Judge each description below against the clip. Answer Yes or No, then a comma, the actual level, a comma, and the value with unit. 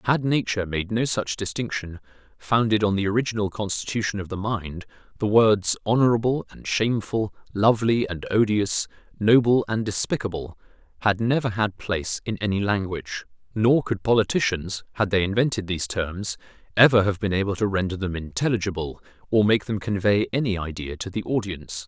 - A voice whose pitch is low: Yes, low, 100 Hz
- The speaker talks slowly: No, average, 155 wpm